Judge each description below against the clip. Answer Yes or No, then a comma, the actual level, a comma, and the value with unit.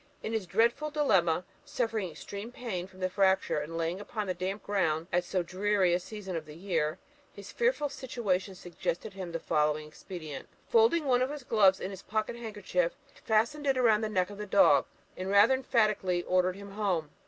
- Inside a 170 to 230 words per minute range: Yes, average, 200 wpm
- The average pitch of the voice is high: Yes, high, 195 Hz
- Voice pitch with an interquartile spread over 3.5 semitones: Yes, average, 4.0 semitones